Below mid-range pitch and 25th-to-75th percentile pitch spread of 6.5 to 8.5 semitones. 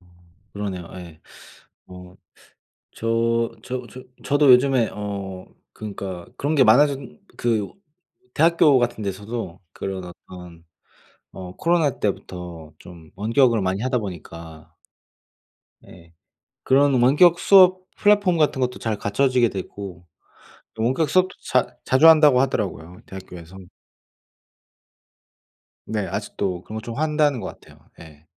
Yes: low, 110 Hz; wide, 6.8 semitones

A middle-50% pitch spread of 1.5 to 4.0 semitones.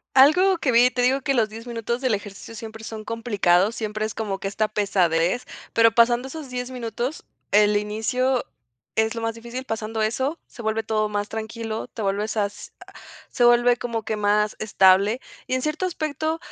Yes: average, 2.9 semitones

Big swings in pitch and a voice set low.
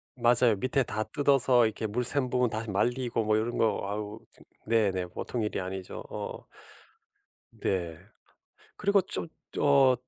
No: average, 3.3 semitones; low, 115 Hz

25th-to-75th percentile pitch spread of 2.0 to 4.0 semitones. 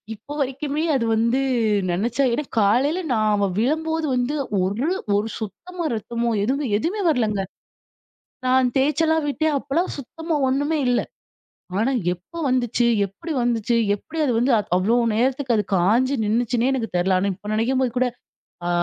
No: average, 4.9 semitones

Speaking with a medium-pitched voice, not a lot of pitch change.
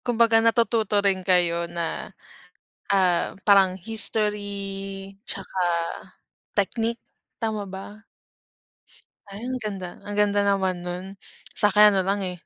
No: high, 200 Hz; narrow, 2.1 semitones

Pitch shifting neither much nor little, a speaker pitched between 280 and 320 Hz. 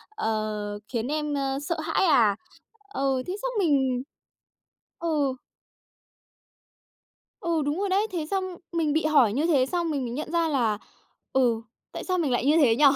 Yes: average, 4.9 semitones; very high, 290 Hz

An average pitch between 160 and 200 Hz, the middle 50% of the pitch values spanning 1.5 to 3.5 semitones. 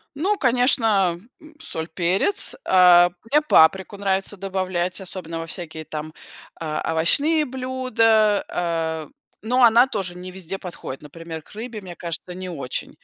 No: medium, 185 Hz; average, 5.3 semitones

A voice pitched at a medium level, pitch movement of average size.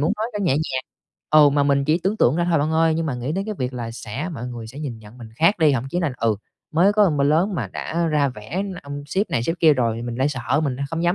Yes: medium, 145 Hz; average, 5.0 semitones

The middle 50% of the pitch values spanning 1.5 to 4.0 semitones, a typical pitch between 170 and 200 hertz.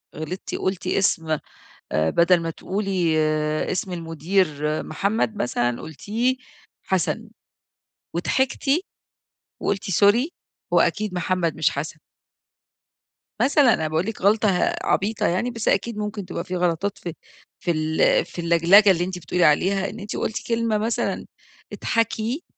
No: average, 4.4 semitones; high, 190 Hz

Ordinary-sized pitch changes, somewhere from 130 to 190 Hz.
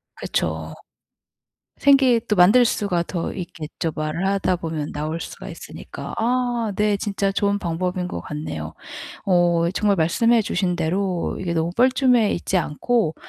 Yes: average, 4.1 semitones; medium, 185 Hz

